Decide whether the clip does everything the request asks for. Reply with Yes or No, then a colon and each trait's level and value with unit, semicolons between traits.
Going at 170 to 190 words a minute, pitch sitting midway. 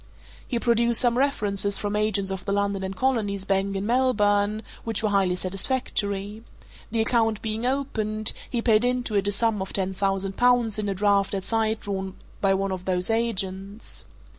No: average, 180 wpm; high, 205 Hz